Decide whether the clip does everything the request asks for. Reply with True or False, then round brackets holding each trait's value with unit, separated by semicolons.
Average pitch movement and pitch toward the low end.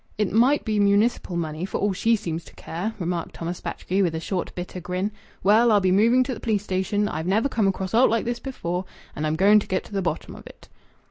False (3.5 semitones; 195 Hz)